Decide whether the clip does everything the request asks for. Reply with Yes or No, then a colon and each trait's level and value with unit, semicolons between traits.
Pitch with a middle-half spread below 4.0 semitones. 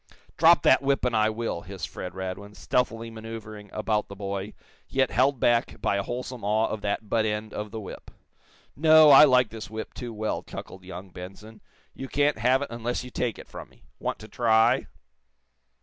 Yes: average, 3.4 semitones